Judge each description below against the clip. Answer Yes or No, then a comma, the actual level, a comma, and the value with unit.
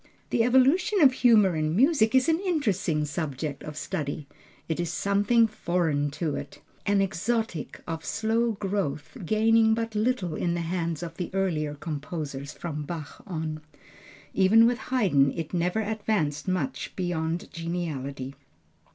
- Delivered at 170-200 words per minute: No, average, 145 wpm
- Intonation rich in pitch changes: Yes, wide, 6.1 semitones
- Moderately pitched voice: Yes, medium, 180 Hz